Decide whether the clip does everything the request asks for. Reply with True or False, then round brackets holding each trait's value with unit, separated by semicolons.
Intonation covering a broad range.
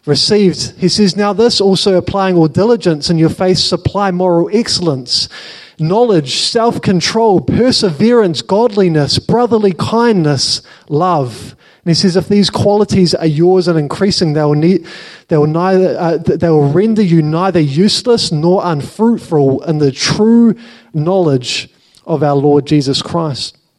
False (4.7 semitones)